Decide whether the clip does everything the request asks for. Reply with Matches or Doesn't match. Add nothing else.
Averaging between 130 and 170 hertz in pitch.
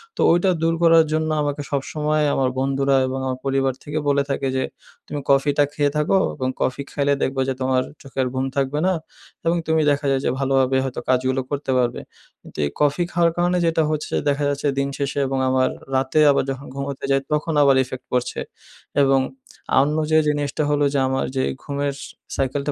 Matches